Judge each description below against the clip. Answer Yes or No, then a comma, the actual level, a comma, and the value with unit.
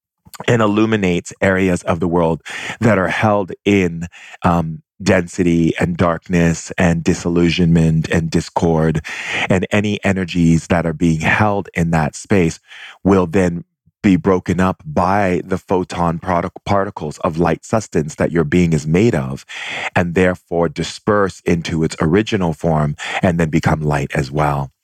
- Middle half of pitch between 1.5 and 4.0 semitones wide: Yes, narrow, 2.4 semitones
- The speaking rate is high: No, average, 145 wpm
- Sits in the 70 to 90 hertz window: Yes, very low, 85 Hz